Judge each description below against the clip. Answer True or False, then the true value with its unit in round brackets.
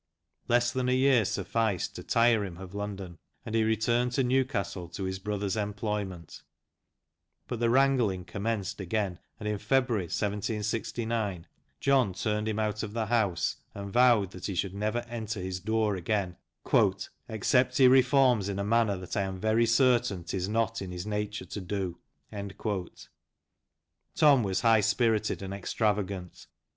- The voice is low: True (105 Hz)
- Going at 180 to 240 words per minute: False (155 wpm)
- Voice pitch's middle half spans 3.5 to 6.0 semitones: False (3.1 semitones)